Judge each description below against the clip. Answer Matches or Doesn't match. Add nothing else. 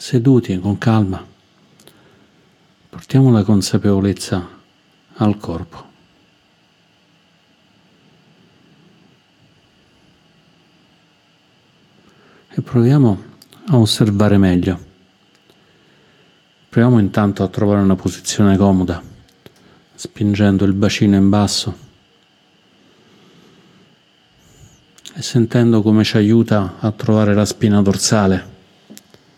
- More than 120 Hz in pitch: Doesn't match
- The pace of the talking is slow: Matches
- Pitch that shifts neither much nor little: Doesn't match